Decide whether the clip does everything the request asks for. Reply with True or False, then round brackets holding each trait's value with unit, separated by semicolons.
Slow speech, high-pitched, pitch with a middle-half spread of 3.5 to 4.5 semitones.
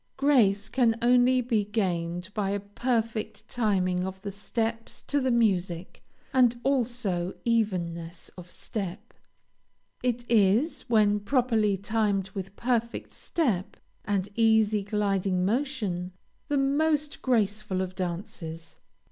True (115 wpm; 210 Hz; 4.0 semitones)